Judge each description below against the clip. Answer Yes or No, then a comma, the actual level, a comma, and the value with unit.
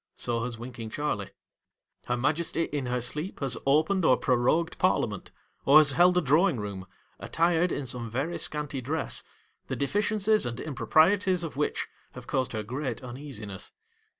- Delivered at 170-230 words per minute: No, average, 155 wpm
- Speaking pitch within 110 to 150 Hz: Yes, medium, 140 Hz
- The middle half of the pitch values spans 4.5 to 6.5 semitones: Yes, average, 5.2 semitones